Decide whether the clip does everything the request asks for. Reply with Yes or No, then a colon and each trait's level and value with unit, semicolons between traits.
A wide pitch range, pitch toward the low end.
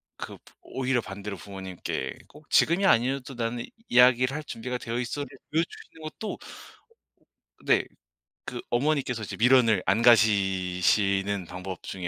No: average, 5.0 semitones; low, 120 Hz